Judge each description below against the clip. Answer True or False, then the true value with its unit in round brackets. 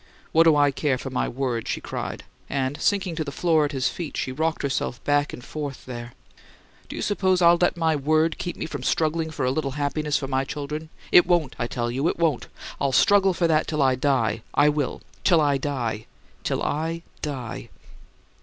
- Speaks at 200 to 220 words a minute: True (205 wpm)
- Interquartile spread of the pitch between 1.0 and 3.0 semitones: False (3.4 semitones)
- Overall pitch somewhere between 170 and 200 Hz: False (145 Hz)